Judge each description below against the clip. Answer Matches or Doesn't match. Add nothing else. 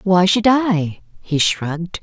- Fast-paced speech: Doesn't match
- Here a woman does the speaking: Matches